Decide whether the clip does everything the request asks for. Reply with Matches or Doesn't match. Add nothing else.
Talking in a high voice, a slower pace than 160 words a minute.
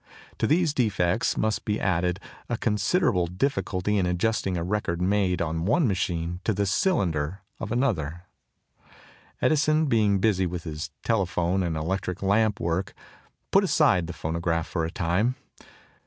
Doesn't match